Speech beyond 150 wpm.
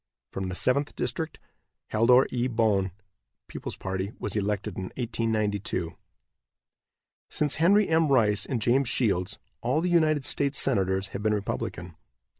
No: slow, 135 wpm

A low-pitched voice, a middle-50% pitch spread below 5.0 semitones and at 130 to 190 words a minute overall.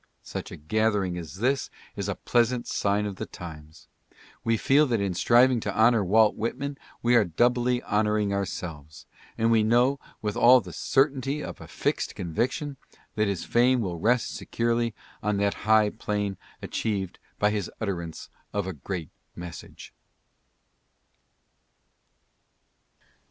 Yes: low, 110 Hz; average, 3.8 semitones; average, 140 wpm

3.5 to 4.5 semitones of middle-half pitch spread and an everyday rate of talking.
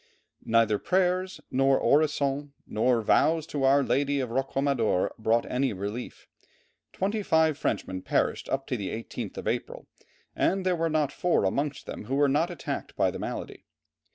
No: average, 5.3 semitones; average, 160 wpm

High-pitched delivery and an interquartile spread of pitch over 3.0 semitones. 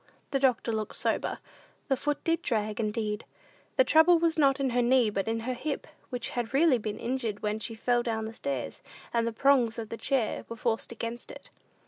Yes: high, 240 Hz; average, 3.5 semitones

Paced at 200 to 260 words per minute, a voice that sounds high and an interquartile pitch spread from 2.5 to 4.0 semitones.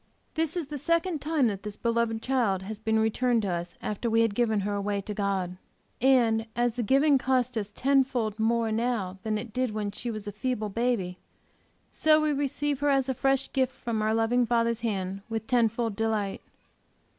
Yes: fast, 205 wpm; high, 230 Hz; average, 3.5 semitones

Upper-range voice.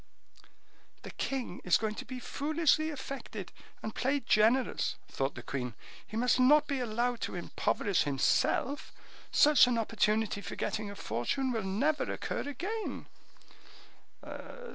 Yes: high, 240 Hz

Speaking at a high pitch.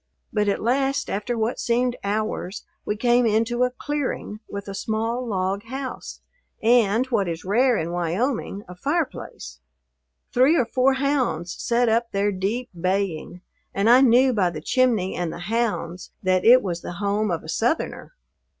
Yes: high, 220 Hz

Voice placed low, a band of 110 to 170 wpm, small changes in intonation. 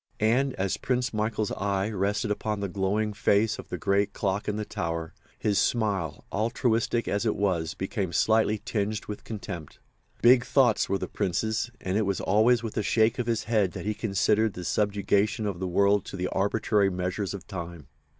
No: low, 105 Hz; average, 190 wpm; narrow, 2.3 semitones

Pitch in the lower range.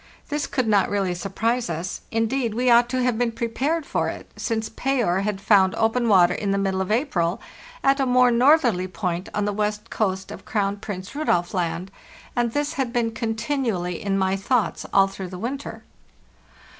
No: high, 215 Hz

